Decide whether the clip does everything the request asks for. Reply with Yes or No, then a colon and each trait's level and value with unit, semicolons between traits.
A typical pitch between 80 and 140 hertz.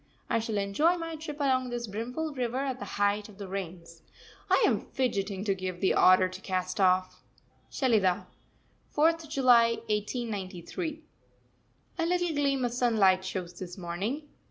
No: high, 220 Hz